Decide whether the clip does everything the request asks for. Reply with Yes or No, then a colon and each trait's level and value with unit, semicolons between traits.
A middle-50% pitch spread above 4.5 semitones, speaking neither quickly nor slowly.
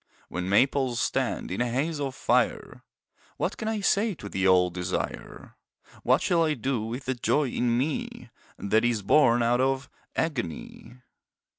Yes: average, 4.9 semitones; average, 160 wpm